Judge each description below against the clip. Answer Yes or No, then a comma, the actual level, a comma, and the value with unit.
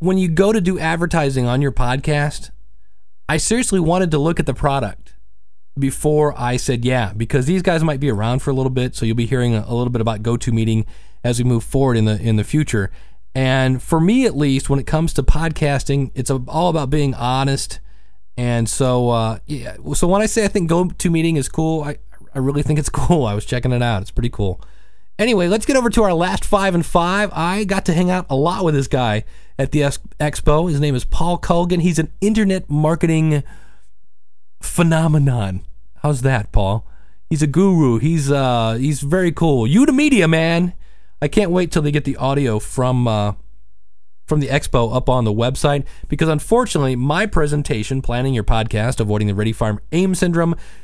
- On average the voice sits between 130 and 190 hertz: Yes, medium, 140 Hz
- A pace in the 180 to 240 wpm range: Yes, average, 200 wpm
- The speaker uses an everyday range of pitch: No, wide, 5.8 semitones